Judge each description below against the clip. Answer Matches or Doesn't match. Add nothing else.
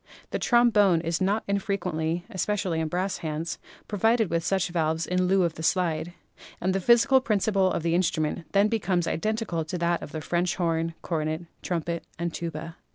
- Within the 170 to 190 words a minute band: Matches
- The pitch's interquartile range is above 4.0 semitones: Doesn't match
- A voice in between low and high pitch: Matches